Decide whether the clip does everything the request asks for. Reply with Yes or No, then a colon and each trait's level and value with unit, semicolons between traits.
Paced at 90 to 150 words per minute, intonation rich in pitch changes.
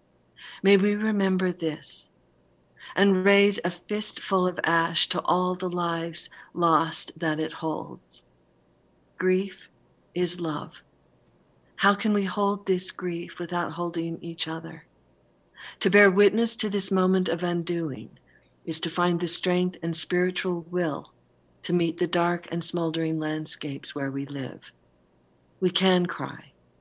No: slow, 135 wpm; narrow, 2.4 semitones